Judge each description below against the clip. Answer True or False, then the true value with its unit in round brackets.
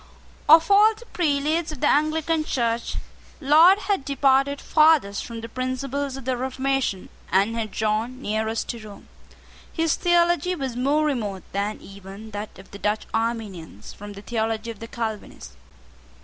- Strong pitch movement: True (5.8 semitones)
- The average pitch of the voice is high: True (250 Hz)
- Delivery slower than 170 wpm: True (155 wpm)